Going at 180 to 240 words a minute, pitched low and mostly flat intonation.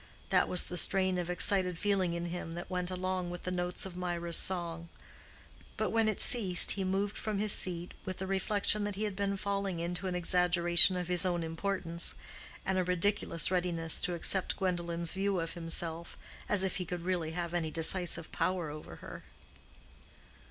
No: average, 185 wpm; medium, 180 Hz; narrow, 1.9 semitones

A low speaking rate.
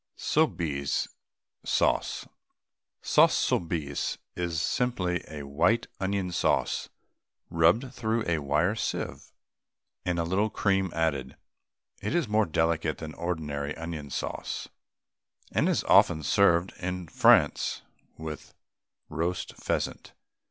Yes: slow, 105 wpm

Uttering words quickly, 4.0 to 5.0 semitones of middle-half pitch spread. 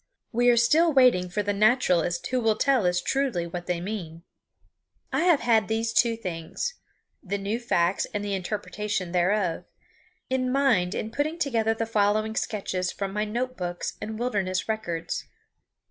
No: average, 160 wpm; average, 4.7 semitones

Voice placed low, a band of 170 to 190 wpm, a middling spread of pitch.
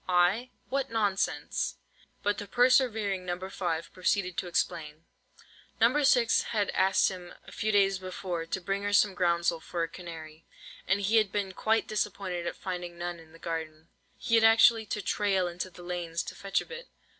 No: high, 190 Hz; average, 180 wpm; average, 3.3 semitones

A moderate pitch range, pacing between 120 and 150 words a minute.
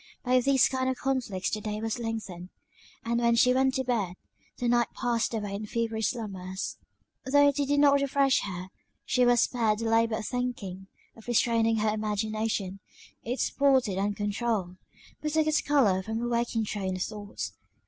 No: average, 3.4 semitones; average, 175 wpm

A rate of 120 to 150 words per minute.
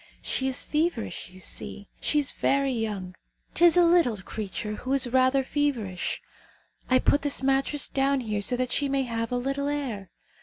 No: average, 180 wpm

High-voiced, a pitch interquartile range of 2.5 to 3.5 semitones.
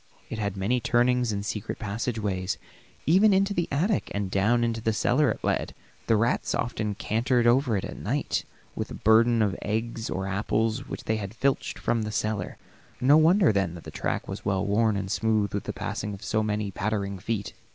No: low, 110 Hz; average, 3.0 semitones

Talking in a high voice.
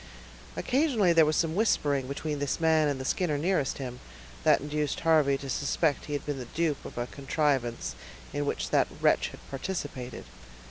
No: medium, 145 Hz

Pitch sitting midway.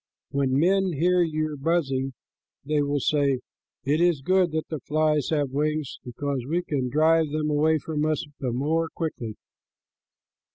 Yes: medium, 150 Hz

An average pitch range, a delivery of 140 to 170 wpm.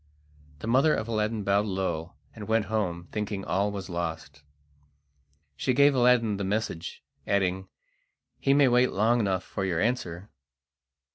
Yes: average, 3.6 semitones; average, 145 wpm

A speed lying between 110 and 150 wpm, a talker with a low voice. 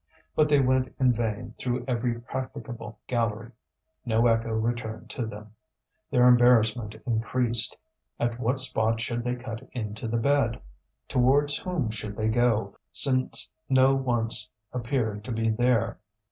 Yes: average, 140 wpm; low, 120 Hz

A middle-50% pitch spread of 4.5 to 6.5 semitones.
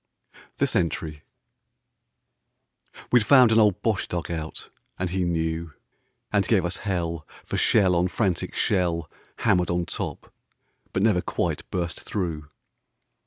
No: average, 3.2 semitones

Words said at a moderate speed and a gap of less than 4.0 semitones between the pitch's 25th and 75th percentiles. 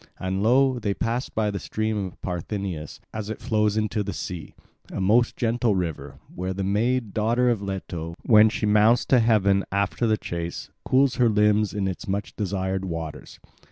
Yes: average, 180 wpm; average, 2.9 semitones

